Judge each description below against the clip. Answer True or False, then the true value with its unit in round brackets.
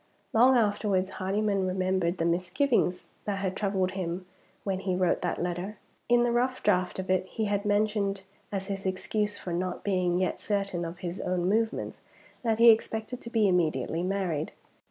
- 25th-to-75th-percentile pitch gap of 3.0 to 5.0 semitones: False (2.5 semitones)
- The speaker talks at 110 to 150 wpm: False (175 wpm)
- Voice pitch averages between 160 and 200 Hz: True (190 Hz)